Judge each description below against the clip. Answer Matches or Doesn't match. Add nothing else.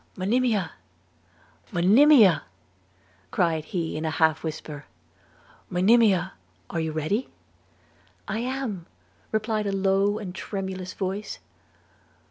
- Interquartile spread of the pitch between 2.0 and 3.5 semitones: Doesn't match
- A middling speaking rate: Doesn't match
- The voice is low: Doesn't match